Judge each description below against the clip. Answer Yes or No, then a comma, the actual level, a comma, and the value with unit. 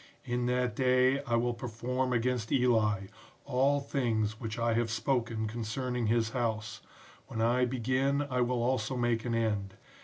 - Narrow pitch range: Yes, narrow, 2.1 semitones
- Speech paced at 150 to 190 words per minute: Yes, average, 155 wpm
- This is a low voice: Yes, low, 120 Hz